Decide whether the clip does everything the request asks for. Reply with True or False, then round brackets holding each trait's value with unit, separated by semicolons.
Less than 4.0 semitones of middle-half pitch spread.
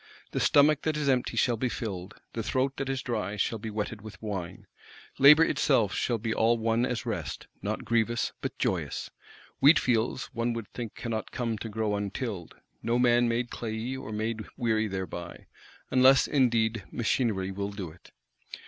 True (2.8 semitones)